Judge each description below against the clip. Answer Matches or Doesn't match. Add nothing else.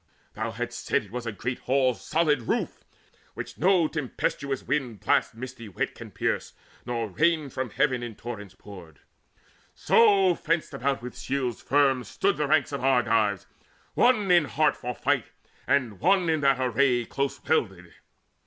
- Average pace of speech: Matches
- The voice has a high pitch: Doesn't match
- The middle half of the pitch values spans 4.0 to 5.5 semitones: Matches